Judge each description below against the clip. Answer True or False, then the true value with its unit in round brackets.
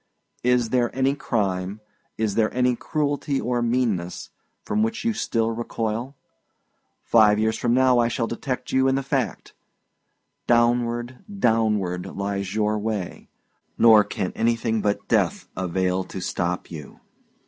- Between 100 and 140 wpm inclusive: True (135 wpm)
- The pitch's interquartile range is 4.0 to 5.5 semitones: False (3.3 semitones)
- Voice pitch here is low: True (115 Hz)